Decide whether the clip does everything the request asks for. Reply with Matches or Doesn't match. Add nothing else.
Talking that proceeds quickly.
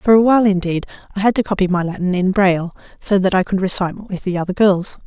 Matches